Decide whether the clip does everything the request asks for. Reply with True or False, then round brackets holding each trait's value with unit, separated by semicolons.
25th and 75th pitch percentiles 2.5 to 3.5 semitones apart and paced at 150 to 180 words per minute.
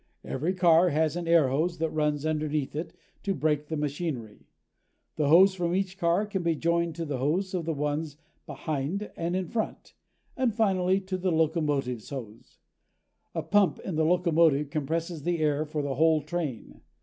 True (3.1 semitones; 175 wpm)